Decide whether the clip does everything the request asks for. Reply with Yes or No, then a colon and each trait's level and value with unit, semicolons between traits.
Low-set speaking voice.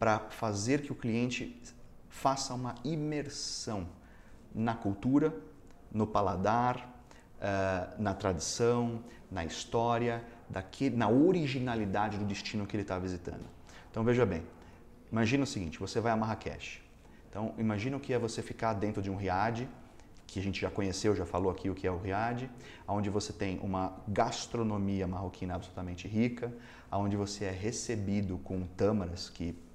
Yes: low, 105 Hz